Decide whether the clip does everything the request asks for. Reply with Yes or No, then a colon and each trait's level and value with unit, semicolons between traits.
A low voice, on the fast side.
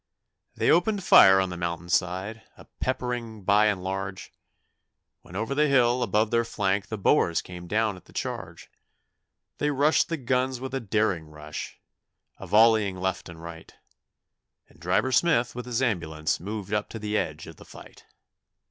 No: low, 105 Hz; average, 170 wpm